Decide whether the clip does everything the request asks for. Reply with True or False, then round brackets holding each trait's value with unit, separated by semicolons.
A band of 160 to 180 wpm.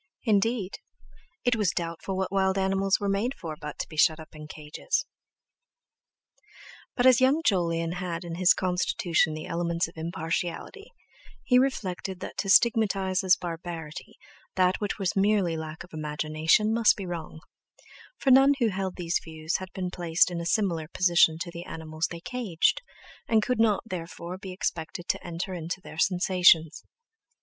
True (165 wpm)